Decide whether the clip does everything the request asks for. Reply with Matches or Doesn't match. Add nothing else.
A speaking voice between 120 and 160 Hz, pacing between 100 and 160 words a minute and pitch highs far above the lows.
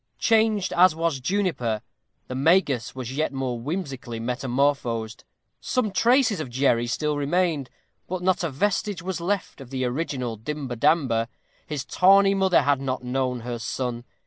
Matches